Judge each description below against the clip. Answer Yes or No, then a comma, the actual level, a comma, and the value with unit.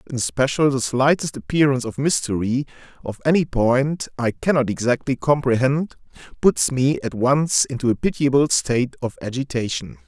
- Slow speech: Yes, slow, 130 wpm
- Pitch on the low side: Yes, low, 130 Hz